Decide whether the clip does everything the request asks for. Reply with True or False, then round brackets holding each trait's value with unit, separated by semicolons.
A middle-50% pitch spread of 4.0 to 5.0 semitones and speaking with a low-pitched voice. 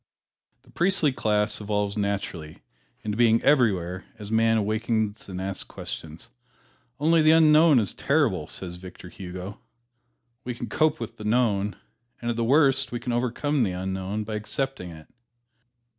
True (4.3 semitones; 110 Hz)